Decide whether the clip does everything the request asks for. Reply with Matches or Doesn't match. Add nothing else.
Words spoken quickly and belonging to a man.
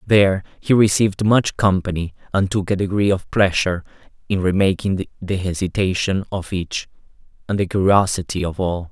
Doesn't match